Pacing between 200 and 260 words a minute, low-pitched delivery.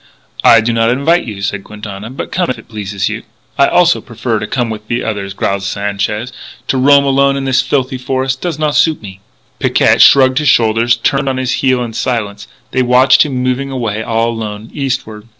Yes: fast, 205 wpm; low, 120 Hz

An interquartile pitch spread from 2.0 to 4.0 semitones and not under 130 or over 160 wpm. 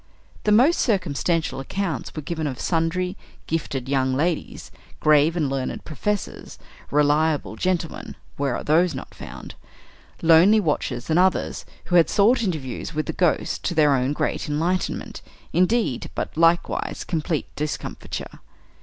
Yes: average, 3.7 semitones; slow, 135 wpm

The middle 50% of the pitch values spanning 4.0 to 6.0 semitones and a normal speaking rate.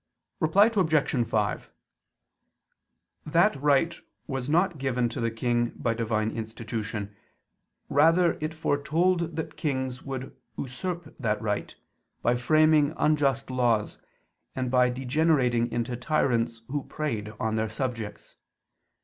No: average, 4.9 semitones; slow, 120 wpm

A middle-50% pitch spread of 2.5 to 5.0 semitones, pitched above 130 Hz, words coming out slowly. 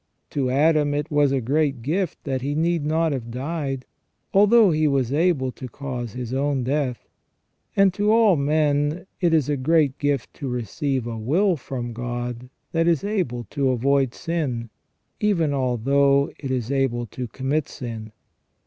No: average, 3.8 semitones; medium, 140 Hz; average, 165 wpm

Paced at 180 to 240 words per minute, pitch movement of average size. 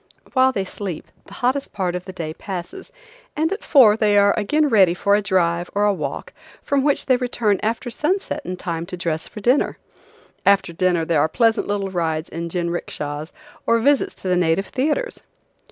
No: average, 190 wpm; wide, 6.1 semitones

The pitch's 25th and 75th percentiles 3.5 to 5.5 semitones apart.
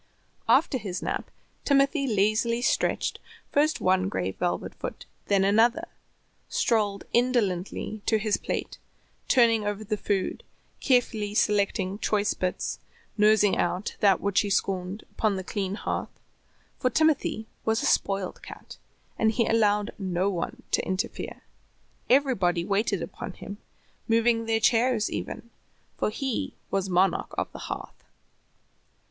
No: average, 3.0 semitones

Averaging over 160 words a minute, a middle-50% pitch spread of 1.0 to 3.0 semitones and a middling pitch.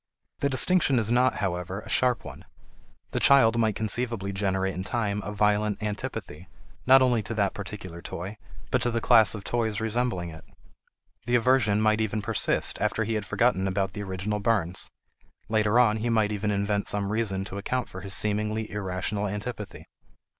No: average, 175 wpm; narrow, 2.6 semitones; low, 105 Hz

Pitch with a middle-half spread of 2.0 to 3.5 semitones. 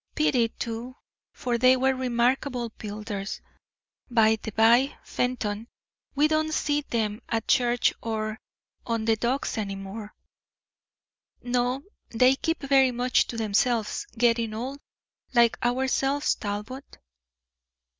Yes: average, 2.8 semitones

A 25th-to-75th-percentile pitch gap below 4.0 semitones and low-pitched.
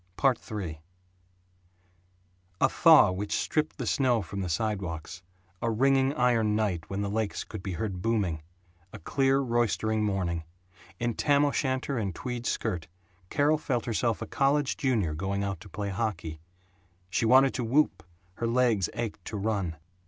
No: average, 4.8 semitones; low, 110 Hz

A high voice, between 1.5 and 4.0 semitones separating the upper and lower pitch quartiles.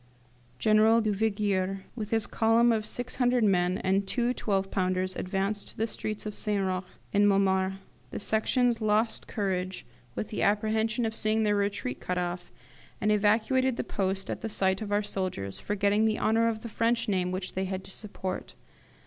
Yes: high, 205 Hz; narrow, 2.6 semitones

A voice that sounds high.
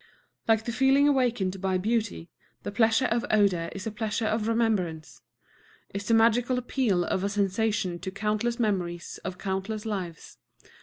Yes: high, 210 Hz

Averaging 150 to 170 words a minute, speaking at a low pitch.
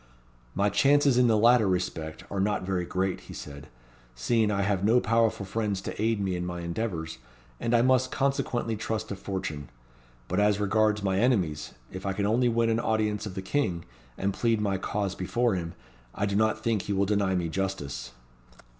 No: average, 195 wpm; low, 100 Hz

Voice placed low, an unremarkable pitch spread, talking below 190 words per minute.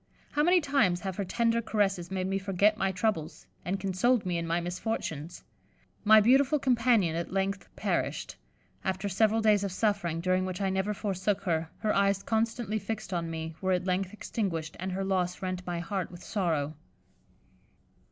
No: high, 190 Hz; average, 3.2 semitones; average, 175 wpm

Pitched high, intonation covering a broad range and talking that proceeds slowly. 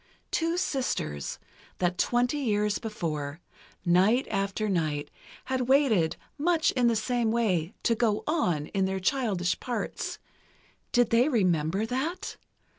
Yes: high, 220 Hz; wide, 5.9 semitones; slow, 125 wpm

